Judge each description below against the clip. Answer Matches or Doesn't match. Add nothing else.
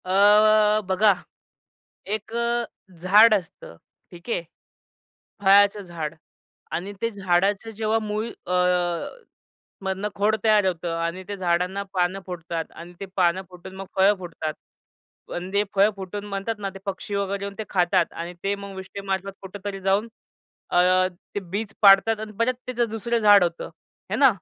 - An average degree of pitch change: Doesn't match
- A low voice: Doesn't match